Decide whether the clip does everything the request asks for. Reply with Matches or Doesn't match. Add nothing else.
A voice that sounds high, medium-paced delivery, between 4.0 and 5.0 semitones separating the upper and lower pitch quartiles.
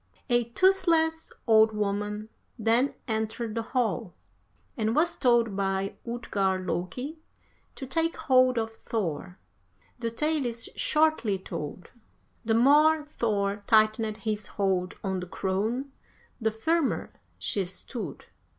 Doesn't match